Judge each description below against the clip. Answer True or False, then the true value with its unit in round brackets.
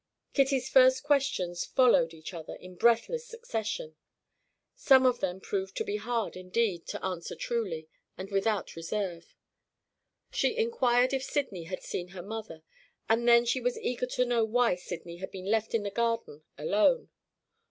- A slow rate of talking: False (160 wpm)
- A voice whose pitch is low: False (225 Hz)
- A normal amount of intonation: False (5.9 semitones)